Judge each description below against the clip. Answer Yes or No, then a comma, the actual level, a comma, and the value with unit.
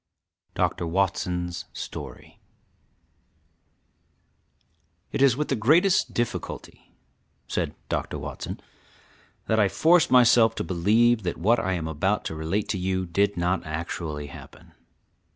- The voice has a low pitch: Yes, very low, 95 Hz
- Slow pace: Yes, slow, 120 wpm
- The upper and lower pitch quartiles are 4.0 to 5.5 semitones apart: Yes, average, 5.2 semitones